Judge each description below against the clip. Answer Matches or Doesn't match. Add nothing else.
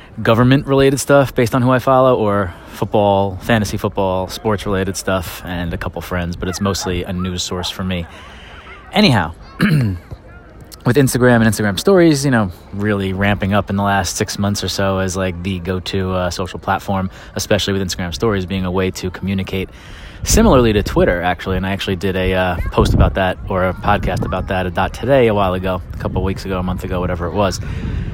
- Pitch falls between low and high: Doesn't match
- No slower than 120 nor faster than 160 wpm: Doesn't match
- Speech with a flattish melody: Matches